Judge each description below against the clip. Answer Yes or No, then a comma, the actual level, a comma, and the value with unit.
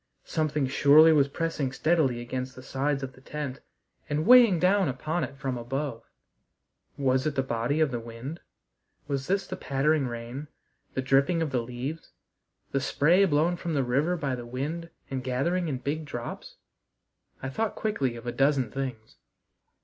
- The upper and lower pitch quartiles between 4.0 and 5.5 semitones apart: No, average, 3.5 semitones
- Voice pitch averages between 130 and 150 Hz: Yes, medium, 140 Hz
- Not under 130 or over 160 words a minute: No, average, 170 wpm